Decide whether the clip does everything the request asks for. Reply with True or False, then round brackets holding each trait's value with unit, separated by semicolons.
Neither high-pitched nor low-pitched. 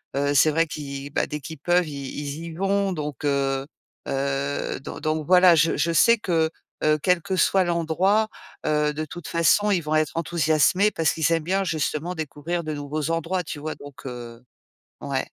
True (155 Hz)